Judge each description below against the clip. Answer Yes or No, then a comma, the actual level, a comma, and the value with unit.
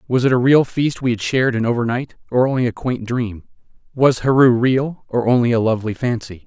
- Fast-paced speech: Yes, fast, 215 wpm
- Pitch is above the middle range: No, low, 120 Hz